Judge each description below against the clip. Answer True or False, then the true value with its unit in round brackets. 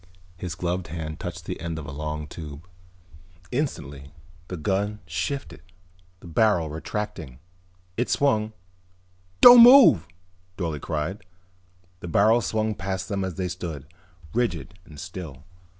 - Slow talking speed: True (130 wpm)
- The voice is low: True (90 Hz)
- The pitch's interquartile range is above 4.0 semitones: True (5.2 semitones)